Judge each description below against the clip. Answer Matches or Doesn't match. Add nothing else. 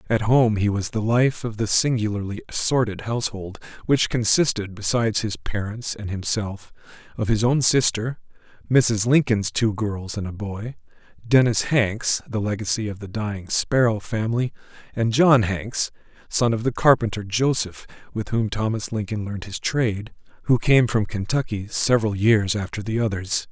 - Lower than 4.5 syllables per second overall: Matches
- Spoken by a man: Matches